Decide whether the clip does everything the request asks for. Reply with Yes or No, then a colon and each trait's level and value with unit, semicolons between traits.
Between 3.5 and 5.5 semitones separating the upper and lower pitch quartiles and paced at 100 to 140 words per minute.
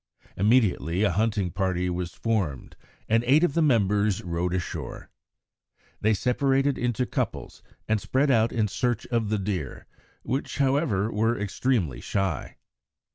Yes: average, 4.8 semitones; slow, 135 wpm